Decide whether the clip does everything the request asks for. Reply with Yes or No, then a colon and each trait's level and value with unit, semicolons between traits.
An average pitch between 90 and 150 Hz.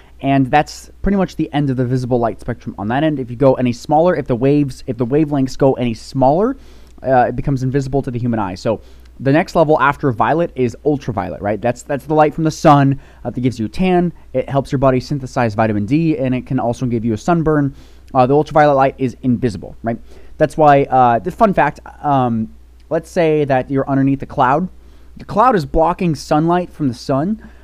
Yes: low, 135 Hz